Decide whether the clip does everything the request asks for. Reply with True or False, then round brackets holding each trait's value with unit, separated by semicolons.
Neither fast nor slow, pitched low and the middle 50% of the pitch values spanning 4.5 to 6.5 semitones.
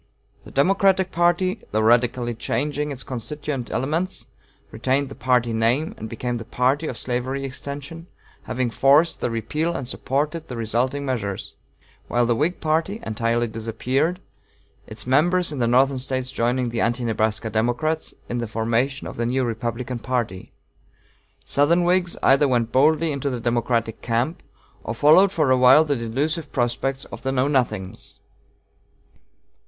False (150 wpm; 130 Hz; 4.0 semitones)